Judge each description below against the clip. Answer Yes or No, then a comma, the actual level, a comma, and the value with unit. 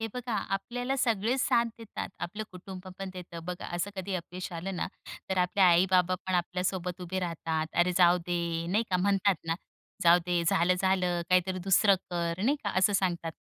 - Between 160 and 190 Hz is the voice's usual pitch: Yes, medium, 185 Hz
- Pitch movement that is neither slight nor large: No, narrow, 2.0 semitones